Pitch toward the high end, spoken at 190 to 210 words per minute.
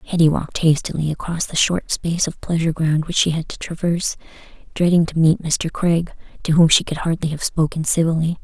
No: medium, 165 Hz; average, 200 wpm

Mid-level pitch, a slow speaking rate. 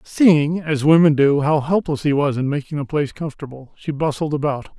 No: medium, 150 Hz; average, 200 wpm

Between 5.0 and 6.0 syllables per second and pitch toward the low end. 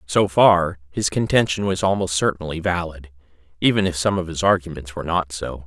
Yes: 5.5 syllables/s; very low, 85 Hz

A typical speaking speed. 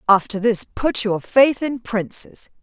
Yes: average, 160 wpm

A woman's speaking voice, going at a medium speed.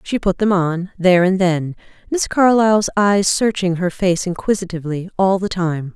Yes: female; average, 170 wpm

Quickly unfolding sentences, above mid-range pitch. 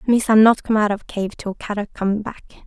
Yes: fast, 225 wpm; high, 210 Hz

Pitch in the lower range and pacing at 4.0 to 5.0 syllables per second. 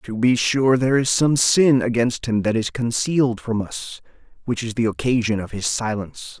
Yes: low, 120 Hz; 4.9 syllables/s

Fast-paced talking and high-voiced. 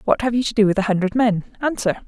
Yes: fast, 260 wpm; high, 215 Hz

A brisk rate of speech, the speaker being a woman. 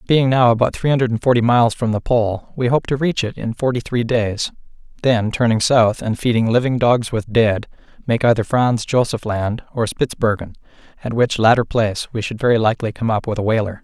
No: fast, 210 wpm; male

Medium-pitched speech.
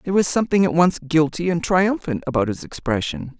Yes: medium, 165 Hz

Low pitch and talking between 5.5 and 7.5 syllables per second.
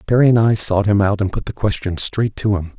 Yes: low, 105 Hz; 5.7 syllables/s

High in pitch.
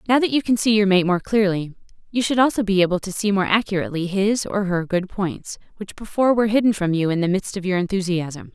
Yes: high, 195 Hz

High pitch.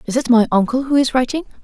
Yes: very high, 250 Hz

